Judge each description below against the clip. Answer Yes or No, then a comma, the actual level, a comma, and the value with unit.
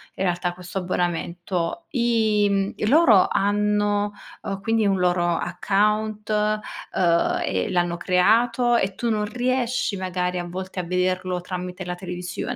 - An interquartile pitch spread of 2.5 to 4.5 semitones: Yes, average, 2.9 semitones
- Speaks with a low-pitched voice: No, high, 190 Hz